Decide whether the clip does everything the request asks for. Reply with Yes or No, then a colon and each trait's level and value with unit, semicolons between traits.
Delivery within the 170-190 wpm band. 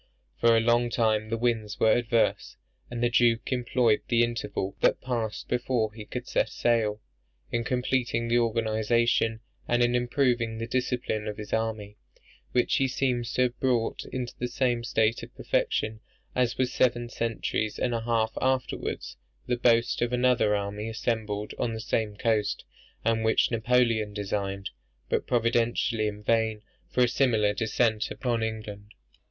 No: average, 160 wpm